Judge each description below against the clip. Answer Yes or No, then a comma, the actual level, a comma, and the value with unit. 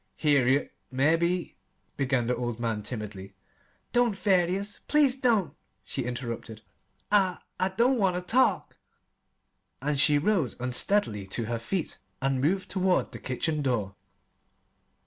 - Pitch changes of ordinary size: No, wide, 7.7 semitones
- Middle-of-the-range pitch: Yes, medium, 145 Hz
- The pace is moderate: No, slow, 130 wpm